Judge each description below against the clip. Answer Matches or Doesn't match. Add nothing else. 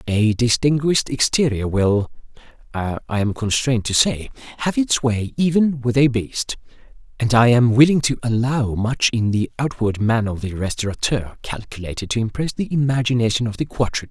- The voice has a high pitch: Doesn't match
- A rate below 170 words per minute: Matches